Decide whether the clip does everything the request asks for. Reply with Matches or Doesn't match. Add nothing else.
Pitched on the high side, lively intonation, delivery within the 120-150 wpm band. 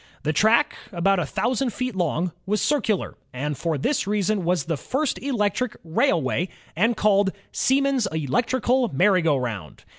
Matches